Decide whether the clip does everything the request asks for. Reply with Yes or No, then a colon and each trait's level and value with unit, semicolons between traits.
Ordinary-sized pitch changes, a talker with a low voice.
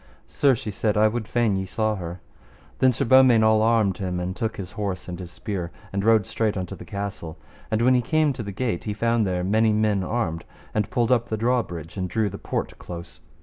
Yes: average, 3.6 semitones; low, 105 Hz